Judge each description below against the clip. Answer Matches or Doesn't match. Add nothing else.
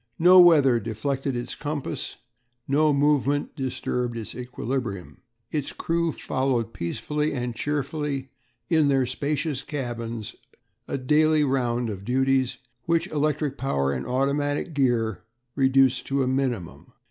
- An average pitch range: Matches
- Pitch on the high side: Doesn't match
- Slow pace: Matches